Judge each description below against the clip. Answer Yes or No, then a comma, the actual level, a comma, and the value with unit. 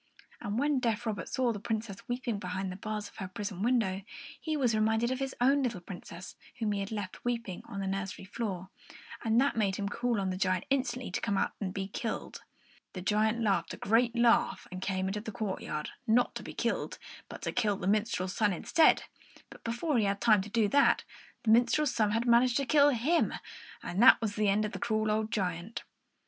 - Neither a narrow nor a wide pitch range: Yes, average, 3.5 semitones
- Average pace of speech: No, fast, 220 wpm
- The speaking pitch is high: Yes, high, 215 Hz